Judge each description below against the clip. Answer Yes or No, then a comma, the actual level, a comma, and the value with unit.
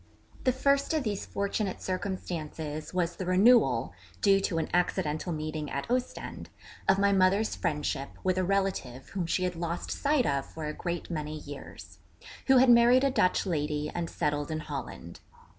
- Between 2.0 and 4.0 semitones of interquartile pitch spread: No, average, 4.7 semitones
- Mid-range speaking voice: Yes, medium, 175 Hz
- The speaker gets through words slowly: No, average, 170 wpm